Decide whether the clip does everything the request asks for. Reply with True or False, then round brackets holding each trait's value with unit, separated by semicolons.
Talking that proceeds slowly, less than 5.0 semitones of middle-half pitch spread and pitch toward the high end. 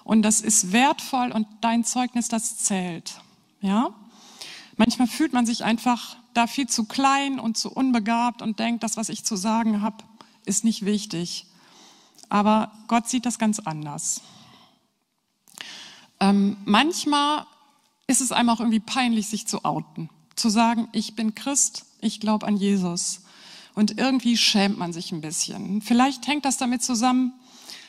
False (155 wpm; 2.9 semitones; 225 Hz)